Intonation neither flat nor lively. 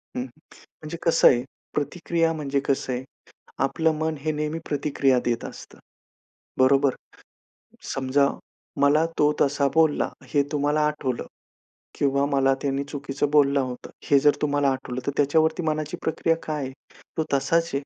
No: narrow, 2.1 semitones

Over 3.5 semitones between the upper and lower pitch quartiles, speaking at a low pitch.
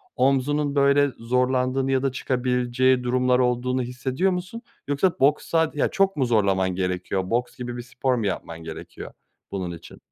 No: narrow, 2.4 semitones; low, 125 Hz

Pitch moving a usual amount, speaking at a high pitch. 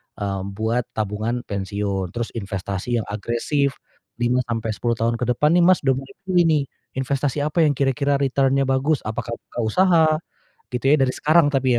No: average, 4.0 semitones; low, 125 Hz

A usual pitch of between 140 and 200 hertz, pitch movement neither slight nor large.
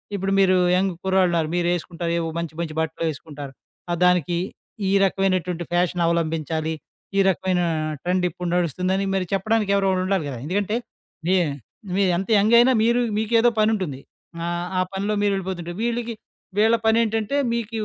Yes: medium, 185 Hz; average, 3.1 semitones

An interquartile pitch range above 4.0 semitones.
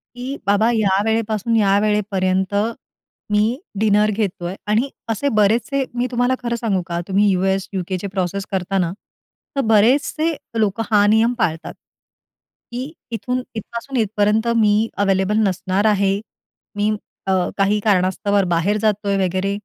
No: average, 2.7 semitones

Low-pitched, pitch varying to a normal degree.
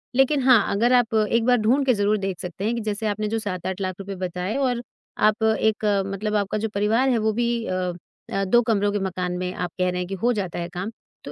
No: high, 210 Hz; average, 3.5 semitones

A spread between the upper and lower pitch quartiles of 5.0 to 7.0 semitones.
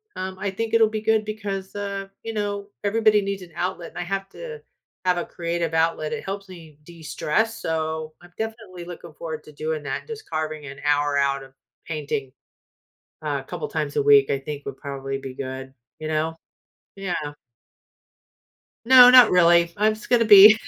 Yes: wide, 5.5 semitones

